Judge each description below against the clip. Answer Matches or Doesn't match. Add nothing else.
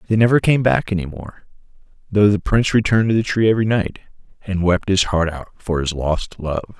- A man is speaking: Matches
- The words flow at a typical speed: Doesn't match